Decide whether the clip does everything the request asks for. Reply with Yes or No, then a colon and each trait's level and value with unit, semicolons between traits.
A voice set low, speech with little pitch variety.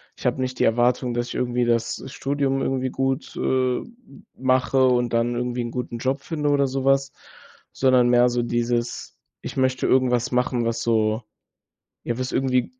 Yes: low, 125 Hz; narrow, 1.5 semitones